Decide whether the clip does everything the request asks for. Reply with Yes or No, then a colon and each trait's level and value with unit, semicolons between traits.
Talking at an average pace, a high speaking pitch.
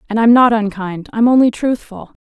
Yes: average, 190 wpm; high, 225 Hz